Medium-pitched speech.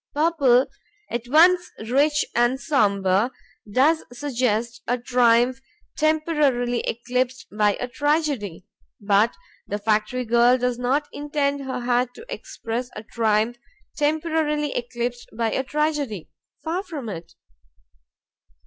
No: very high, 250 Hz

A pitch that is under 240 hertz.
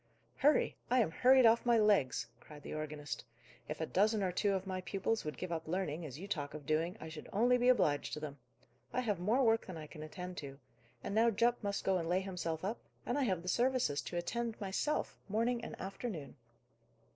Yes: high, 190 Hz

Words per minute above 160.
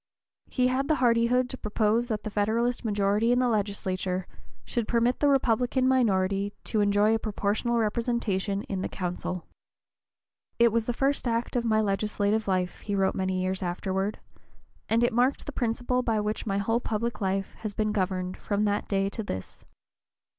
Yes: average, 175 wpm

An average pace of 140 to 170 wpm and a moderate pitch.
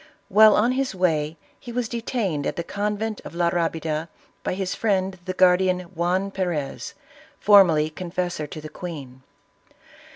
Yes: average, 150 wpm; medium, 180 Hz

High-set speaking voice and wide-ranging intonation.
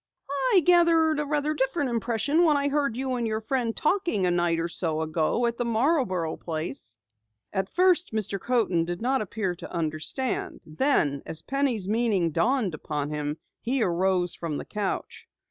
Yes: high, 220 Hz; wide, 8.2 semitones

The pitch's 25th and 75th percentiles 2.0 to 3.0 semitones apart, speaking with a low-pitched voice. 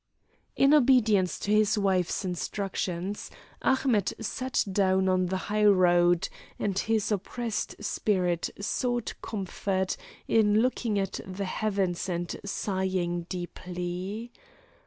No: average, 2.7 semitones; high, 195 Hz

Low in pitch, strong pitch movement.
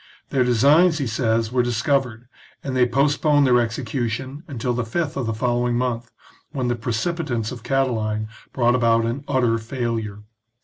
No: low, 120 Hz; average, 2.8 semitones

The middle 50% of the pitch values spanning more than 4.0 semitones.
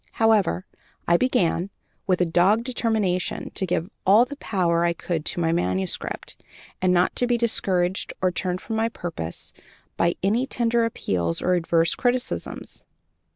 Yes: average, 4.9 semitones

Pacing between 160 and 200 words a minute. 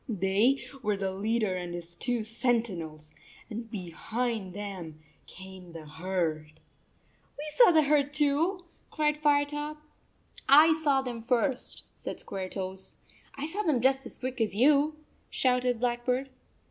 No: slow, 135 wpm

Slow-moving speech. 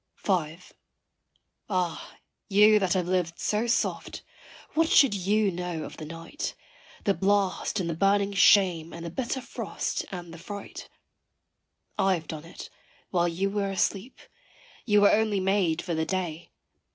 No: average, 150 wpm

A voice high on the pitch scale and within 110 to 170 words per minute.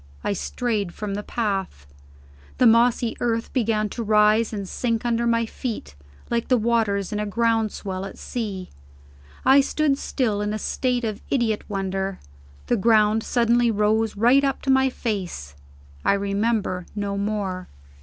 Yes: high, 220 Hz; average, 155 wpm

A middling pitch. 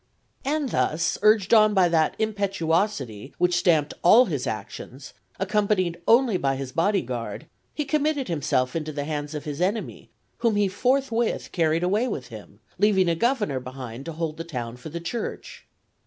Yes: medium, 170 Hz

